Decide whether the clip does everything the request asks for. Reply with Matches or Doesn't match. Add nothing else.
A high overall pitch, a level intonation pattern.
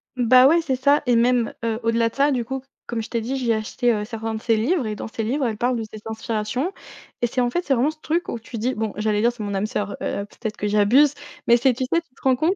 Doesn't match